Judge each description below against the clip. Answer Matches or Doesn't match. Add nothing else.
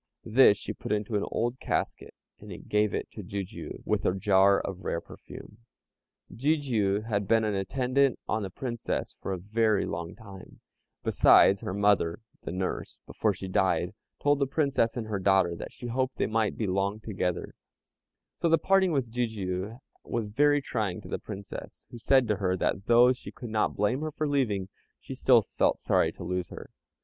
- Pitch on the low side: Matches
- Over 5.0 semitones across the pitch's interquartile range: Doesn't match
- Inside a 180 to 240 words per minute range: Matches